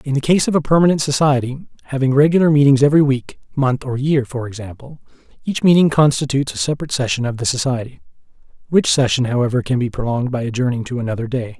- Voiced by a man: Yes, male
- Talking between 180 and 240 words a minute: Yes, average, 190 wpm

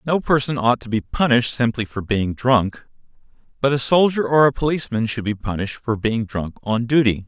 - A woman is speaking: No, male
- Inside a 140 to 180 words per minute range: No, average, 200 wpm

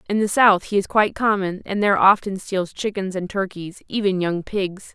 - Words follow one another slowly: No, fast, 205 wpm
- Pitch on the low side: No, high, 195 Hz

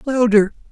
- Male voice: Yes, male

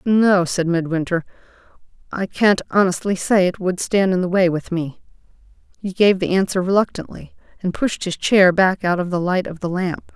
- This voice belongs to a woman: Yes, female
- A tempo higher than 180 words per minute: Yes, average, 190 wpm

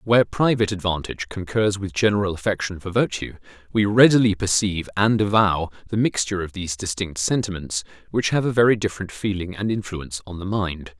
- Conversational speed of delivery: Yes, average, 170 wpm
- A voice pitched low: Yes, low, 100 Hz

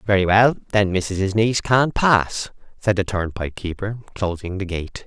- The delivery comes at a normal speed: Yes, average, 165 wpm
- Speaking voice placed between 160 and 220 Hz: No, low, 100 Hz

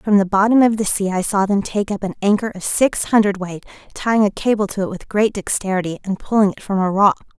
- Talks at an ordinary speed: No, fast, 245 wpm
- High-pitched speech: Yes, high, 200 Hz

